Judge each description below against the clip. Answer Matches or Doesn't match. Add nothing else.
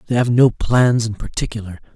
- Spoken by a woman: Doesn't match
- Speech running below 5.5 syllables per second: Doesn't match